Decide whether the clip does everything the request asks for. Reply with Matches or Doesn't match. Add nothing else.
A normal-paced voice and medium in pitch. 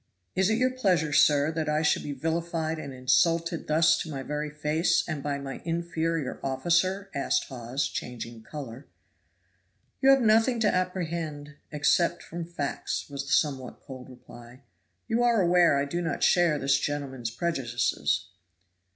Matches